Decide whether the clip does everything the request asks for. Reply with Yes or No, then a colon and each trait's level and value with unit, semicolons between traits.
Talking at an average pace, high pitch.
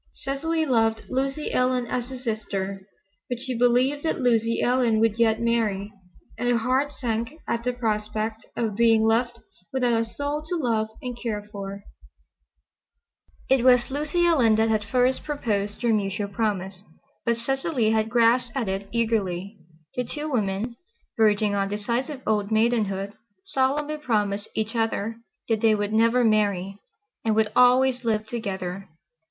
Yes: average, 150 wpm; high, 230 Hz